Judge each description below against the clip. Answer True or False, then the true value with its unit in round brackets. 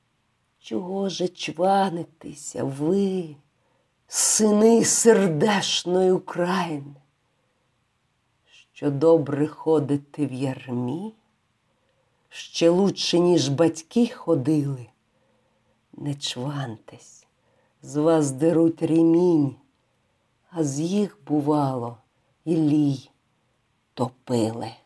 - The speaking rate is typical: False (70 wpm)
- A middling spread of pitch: True (4.4 semitones)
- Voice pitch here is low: False (150 Hz)